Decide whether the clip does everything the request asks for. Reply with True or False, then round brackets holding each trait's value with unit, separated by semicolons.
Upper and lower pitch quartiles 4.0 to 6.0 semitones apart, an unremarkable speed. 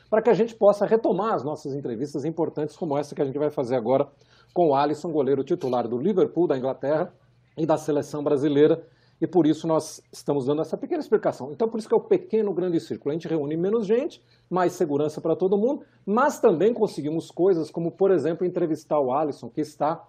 False (5.3 semitones; 210 wpm)